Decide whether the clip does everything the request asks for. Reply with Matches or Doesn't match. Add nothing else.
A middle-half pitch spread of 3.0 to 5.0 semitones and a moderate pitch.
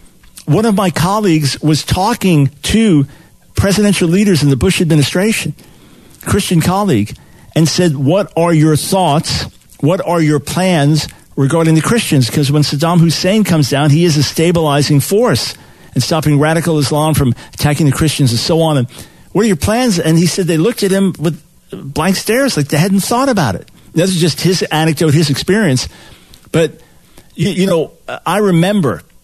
Matches